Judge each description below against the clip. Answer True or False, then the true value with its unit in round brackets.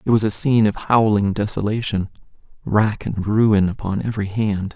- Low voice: True (105 Hz)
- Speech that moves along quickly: False (165 wpm)